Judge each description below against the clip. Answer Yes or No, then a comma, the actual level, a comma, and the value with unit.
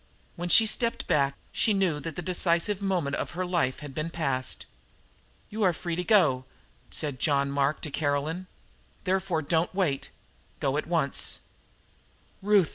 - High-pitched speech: No, medium, 165 Hz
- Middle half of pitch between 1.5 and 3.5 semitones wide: No, average, 4.6 semitones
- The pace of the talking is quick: No, average, 155 wpm